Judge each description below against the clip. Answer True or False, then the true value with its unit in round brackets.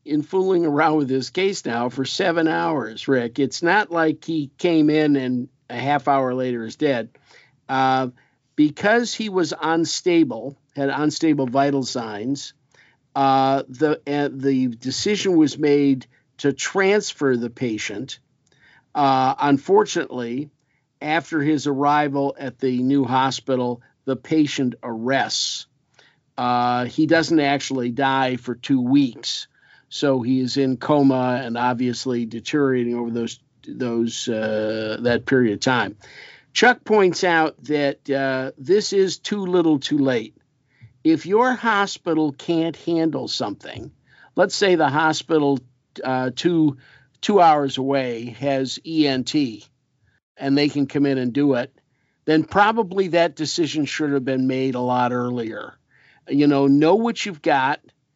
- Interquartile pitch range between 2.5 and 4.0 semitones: True (3.6 semitones)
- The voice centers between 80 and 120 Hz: False (140 Hz)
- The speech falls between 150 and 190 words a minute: False (135 wpm)